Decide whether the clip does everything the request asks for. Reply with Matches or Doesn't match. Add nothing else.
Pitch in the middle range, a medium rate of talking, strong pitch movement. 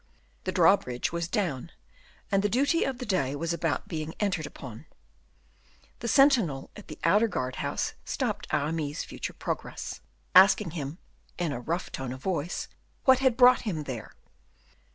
Matches